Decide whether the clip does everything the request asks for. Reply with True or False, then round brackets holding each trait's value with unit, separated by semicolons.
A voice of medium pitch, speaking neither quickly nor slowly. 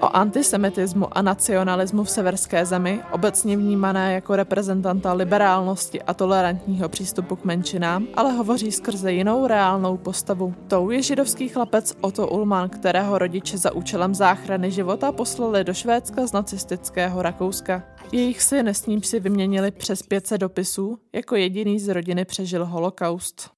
False (195 Hz; 145 wpm)